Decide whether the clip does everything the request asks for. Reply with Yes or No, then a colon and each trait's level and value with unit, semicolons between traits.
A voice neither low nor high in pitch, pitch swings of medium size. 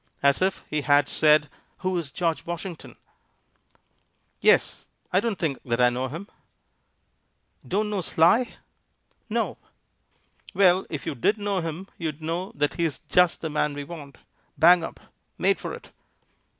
Yes: medium, 165 Hz; average, 4.1 semitones